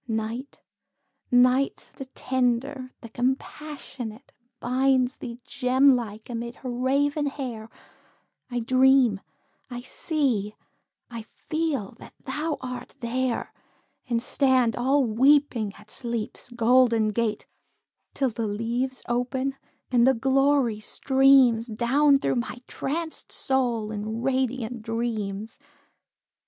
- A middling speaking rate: No, slow, 110 wpm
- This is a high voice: Yes, very high, 250 Hz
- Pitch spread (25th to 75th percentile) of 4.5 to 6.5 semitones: No, average, 2.7 semitones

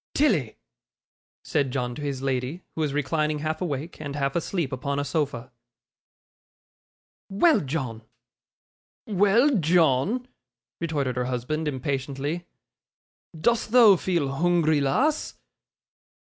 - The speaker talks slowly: Yes, slow, 110 wpm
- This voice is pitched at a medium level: Yes, medium, 150 Hz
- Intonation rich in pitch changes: No, average, 4.5 semitones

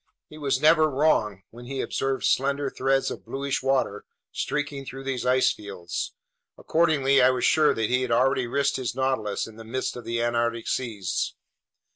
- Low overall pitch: Yes, low, 130 Hz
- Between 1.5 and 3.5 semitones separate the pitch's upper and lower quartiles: Yes, average, 2.8 semitones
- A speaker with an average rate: Yes, average, 175 wpm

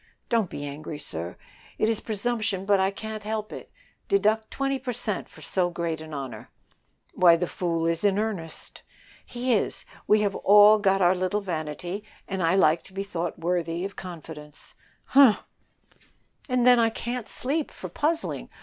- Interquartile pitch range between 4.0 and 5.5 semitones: Yes, average, 4.7 semitones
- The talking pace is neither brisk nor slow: Yes, average, 165 wpm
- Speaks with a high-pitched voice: Yes, high, 195 Hz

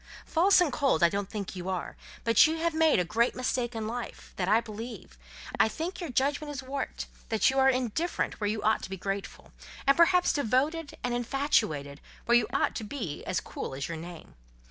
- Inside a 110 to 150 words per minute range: No, average, 195 wpm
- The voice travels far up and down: Yes, wide, 6.0 semitones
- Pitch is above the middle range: Yes, high, 240 Hz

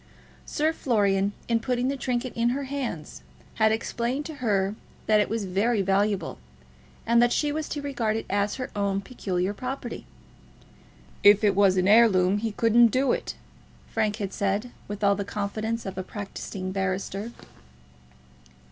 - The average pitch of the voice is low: No, high, 215 Hz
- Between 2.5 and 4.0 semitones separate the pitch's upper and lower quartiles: Yes, average, 3.3 semitones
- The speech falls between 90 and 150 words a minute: No, average, 160 wpm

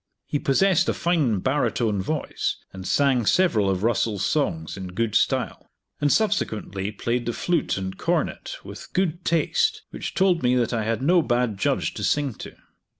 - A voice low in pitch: Yes, low, 125 Hz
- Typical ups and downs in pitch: No, wide, 7.3 semitones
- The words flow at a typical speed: Yes, average, 170 wpm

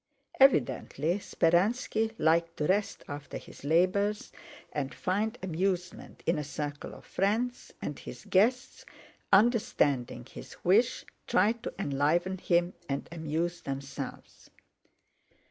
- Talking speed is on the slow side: Yes, slow, 110 wpm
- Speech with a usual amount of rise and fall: No, wide, 5.7 semitones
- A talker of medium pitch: Yes, medium, 175 Hz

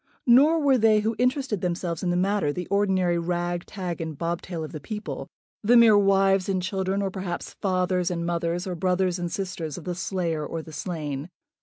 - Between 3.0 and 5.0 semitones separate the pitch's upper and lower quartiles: No, narrow, 2.5 semitones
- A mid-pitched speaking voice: Yes, medium, 180 Hz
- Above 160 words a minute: Yes, average, 195 wpm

